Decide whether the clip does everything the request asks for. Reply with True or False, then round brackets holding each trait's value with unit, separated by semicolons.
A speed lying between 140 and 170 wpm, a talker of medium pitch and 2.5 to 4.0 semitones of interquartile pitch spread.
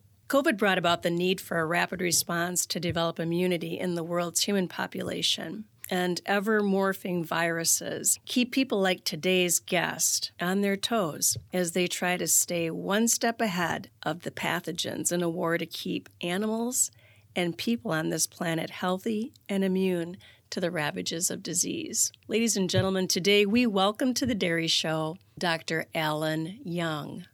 True (160 wpm; 180 Hz; 3.1 semitones)